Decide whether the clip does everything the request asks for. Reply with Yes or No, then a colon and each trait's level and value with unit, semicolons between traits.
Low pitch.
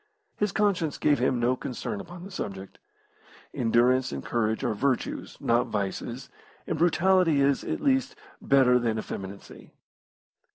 Yes: low, 130 Hz